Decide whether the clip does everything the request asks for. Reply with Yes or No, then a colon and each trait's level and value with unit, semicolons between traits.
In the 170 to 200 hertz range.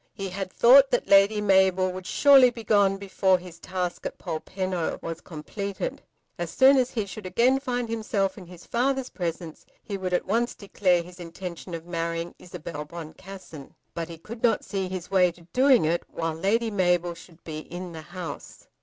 Yes: medium, 185 Hz